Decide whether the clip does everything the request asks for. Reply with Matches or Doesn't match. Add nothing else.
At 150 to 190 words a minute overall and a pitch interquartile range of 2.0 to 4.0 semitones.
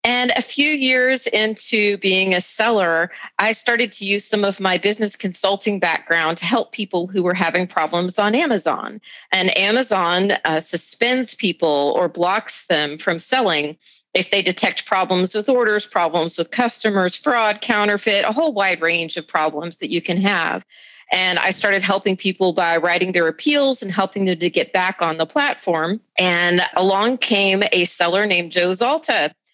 Matches